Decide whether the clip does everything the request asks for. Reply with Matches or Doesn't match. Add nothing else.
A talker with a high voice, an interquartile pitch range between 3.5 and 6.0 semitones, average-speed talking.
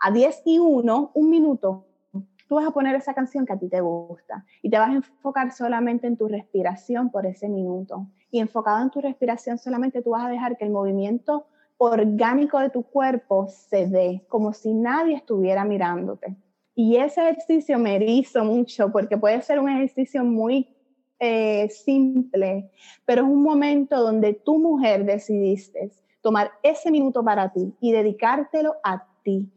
Matches